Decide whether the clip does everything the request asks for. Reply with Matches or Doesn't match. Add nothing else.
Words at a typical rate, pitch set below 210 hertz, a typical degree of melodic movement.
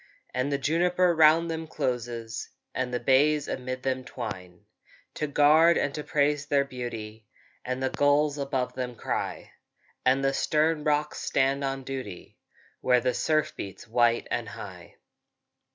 Matches